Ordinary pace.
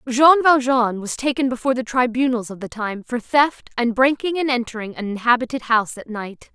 Yes: average, 190 wpm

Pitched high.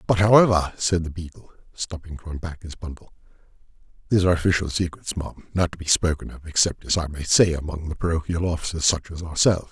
No: very low, 85 Hz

